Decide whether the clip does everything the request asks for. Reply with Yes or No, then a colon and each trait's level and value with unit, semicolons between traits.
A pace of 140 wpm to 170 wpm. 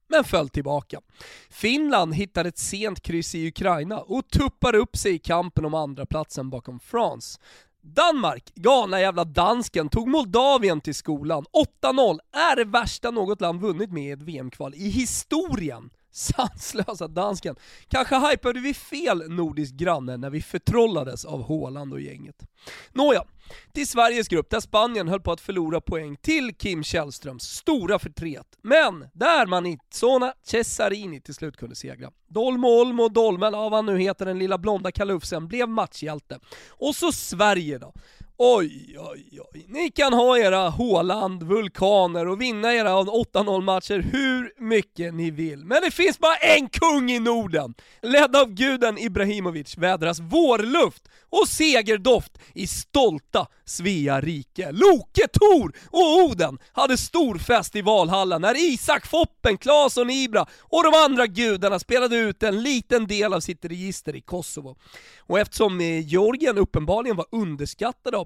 Yes: average, 150 wpm